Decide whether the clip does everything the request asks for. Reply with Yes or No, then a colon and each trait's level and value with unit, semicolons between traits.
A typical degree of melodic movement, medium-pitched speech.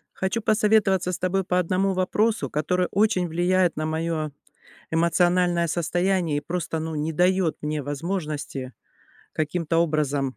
Yes: average, 3.0 semitones; medium, 175 Hz